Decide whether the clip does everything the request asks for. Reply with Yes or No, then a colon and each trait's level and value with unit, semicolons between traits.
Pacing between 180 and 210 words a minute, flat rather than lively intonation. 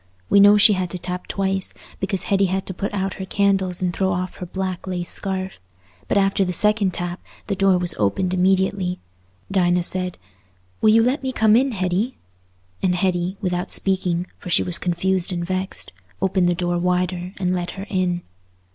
Yes: average, 190 wpm; narrow, 1.5 semitones